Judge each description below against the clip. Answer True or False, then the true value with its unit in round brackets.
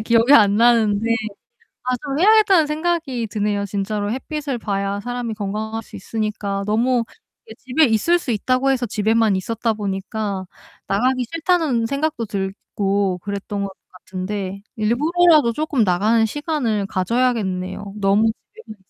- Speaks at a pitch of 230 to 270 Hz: False (220 Hz)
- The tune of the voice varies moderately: True (4.1 semitones)